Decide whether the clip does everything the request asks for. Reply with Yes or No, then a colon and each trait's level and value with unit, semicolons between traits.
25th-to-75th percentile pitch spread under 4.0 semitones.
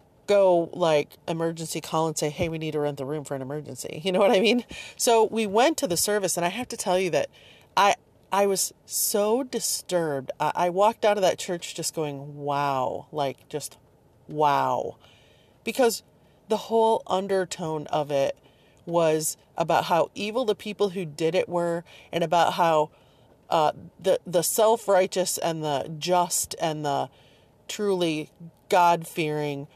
No: average, 4.3 semitones